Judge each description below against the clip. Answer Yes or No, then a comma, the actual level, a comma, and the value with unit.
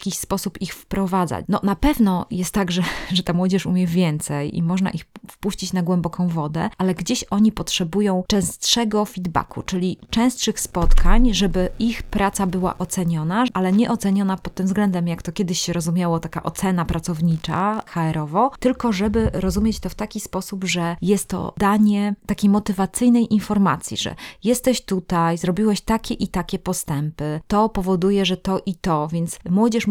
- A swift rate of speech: Yes, fast, 165 wpm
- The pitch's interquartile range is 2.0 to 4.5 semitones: Yes, average, 2.8 semitones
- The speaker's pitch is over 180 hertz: Yes, high, 190 Hz